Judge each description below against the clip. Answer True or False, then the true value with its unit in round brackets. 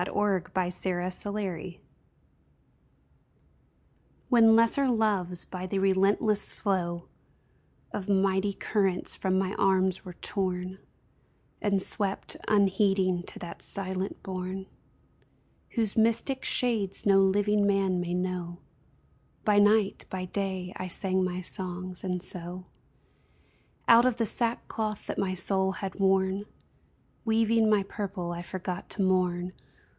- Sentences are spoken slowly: True (120 wpm)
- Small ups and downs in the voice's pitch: True (2.0 semitones)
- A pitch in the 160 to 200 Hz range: True (190 Hz)